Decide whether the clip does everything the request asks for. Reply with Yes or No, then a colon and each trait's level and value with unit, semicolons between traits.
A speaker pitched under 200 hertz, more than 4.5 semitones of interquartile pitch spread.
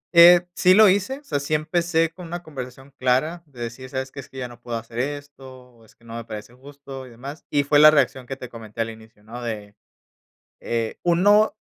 Yes: low, 135 Hz; average, 5.2 semitones